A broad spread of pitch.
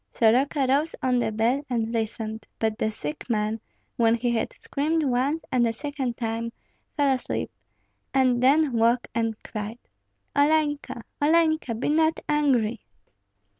No: average, 4.2 semitones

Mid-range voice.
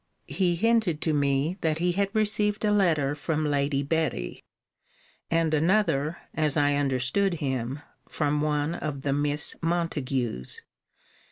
Yes: medium, 150 Hz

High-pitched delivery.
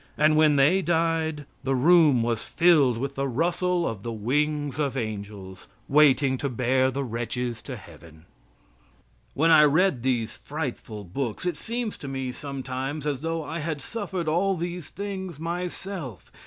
No: medium, 145 Hz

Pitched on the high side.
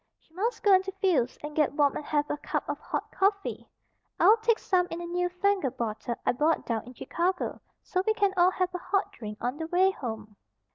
Yes: very high, 350 Hz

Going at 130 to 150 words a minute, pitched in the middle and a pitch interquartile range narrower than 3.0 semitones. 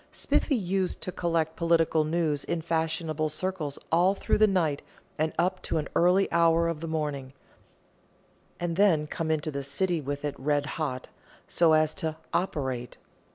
No: average, 160 wpm; medium, 160 Hz; narrow, 2.5 semitones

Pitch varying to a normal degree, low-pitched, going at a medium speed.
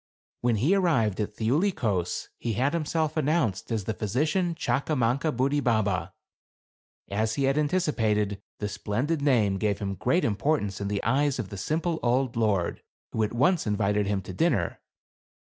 No: wide, 6.2 semitones; low, 115 Hz; average, 160 wpm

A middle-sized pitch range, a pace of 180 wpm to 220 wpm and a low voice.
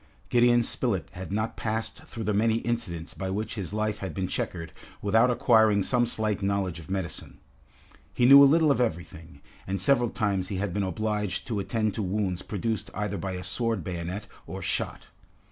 Yes: average, 3.3 semitones; average, 185 wpm; low, 105 Hz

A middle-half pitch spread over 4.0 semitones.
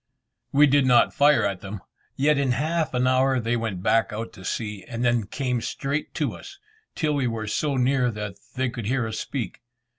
No: average, 3.7 semitones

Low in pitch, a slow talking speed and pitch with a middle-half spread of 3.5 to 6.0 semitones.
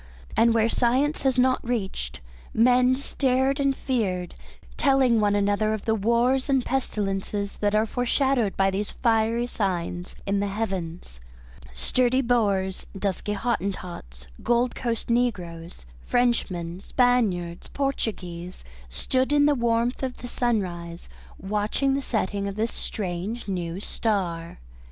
No: high, 220 Hz; slow, 130 wpm; average, 4.6 semitones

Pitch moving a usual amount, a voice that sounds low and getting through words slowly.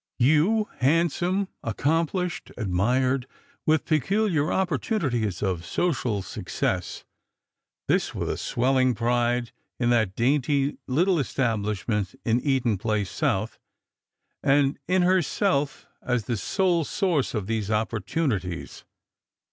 No: wide, 6.6 semitones; low, 130 Hz; slow, 110 wpm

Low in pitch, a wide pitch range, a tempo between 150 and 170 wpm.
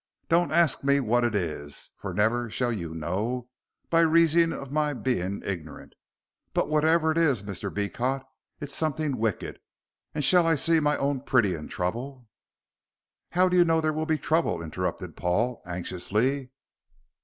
Yes: low, 130 Hz; wide, 7.6 semitones; average, 160 wpm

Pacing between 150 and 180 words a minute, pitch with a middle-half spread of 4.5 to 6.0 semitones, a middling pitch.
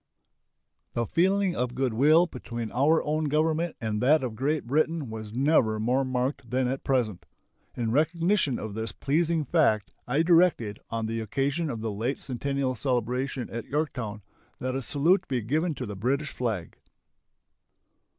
No: average, 160 wpm; average, 5.1 semitones; low, 130 Hz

